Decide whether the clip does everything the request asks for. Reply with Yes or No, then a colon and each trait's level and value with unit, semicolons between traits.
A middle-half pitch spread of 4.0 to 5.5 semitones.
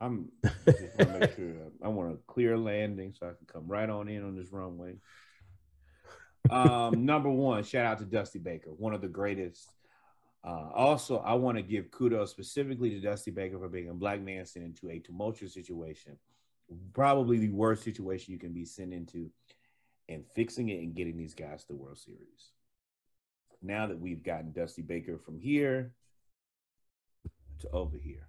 Yes: average, 4.6 semitones